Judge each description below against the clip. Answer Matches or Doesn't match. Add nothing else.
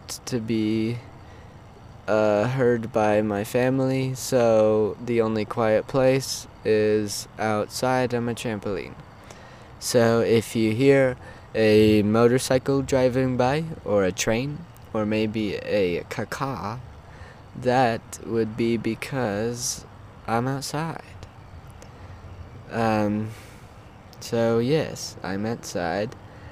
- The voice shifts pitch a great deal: Doesn't match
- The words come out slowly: Matches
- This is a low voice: Matches